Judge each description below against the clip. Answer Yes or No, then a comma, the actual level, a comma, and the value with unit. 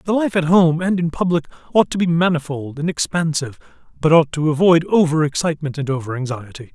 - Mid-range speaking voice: Yes, medium, 160 Hz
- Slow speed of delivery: No, average, 195 wpm